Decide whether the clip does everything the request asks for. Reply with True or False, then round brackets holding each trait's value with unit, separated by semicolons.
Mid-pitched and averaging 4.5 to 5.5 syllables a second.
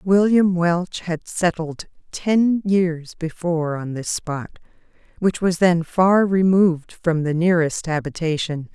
False (170 Hz; 3.9 syllables/s)